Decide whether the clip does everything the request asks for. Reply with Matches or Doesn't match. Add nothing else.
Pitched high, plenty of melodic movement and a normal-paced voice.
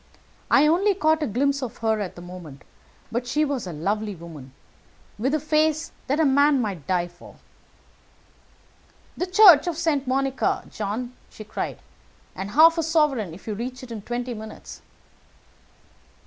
Matches